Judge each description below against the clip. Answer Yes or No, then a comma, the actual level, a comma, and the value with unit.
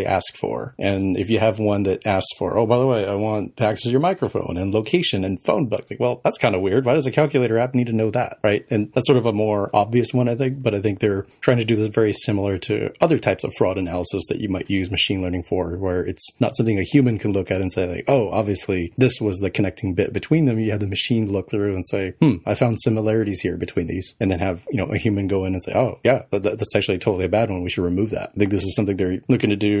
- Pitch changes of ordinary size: Yes, average, 3.2 semitones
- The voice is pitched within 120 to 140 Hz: No, low, 105 Hz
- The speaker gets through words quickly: Yes, fast, 285 wpm